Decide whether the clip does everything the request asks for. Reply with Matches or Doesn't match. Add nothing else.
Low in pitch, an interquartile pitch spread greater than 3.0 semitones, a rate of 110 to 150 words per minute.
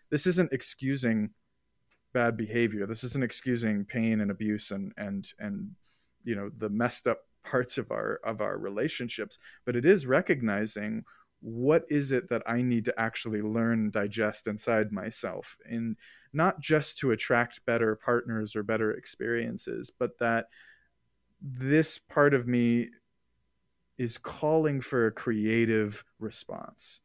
Matches